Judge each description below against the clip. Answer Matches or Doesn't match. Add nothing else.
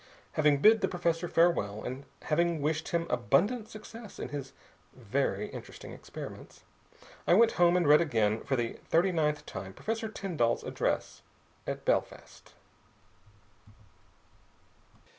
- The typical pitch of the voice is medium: Matches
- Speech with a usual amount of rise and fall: Doesn't match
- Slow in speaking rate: Matches